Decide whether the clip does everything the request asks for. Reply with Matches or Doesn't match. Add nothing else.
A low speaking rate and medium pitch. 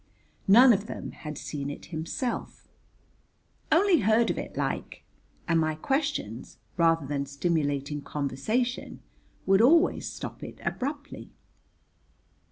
Matches